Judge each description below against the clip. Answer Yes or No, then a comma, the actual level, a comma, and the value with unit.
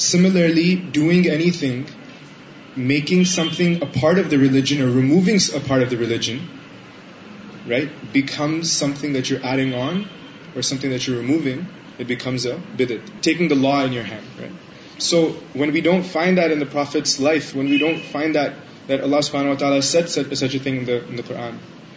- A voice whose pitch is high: No, medium, 145 Hz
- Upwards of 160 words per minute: No, average, 150 wpm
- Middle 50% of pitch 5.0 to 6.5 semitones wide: No, average, 3.5 semitones